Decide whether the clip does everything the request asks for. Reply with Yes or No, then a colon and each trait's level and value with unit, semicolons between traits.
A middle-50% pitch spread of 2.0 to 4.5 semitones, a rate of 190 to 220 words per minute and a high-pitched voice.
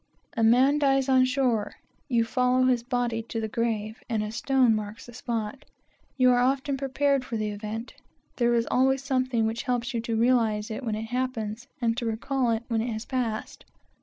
Yes: narrow, 2.5 semitones; average, 195 wpm; high, 240 Hz